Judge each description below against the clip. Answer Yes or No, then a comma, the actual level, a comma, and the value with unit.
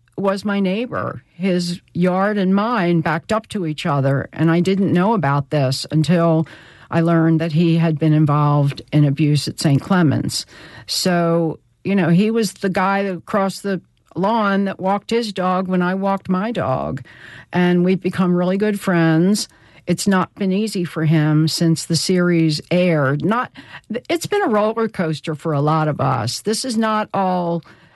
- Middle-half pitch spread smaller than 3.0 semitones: No, average, 3.7 semitones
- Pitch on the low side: No, medium, 175 Hz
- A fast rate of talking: No, average, 175 wpm